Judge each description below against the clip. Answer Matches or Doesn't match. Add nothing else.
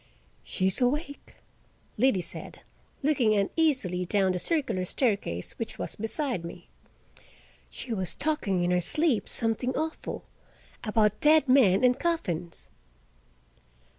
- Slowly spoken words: Matches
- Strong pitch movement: Matches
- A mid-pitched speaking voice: Doesn't match